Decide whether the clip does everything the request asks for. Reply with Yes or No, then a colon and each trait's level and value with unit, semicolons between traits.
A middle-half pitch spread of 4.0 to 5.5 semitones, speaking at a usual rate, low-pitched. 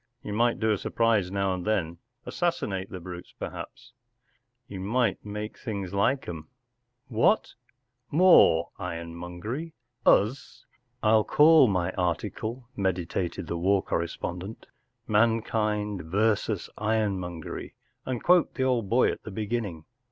No: average, 4.3 semitones; slow, 130 wpm; low, 105 Hz